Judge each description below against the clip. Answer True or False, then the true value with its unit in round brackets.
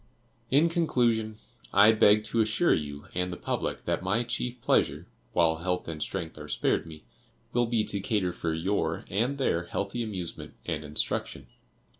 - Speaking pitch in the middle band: False (100 Hz)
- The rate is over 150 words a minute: True (165 wpm)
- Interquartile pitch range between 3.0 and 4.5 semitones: False (5.6 semitones)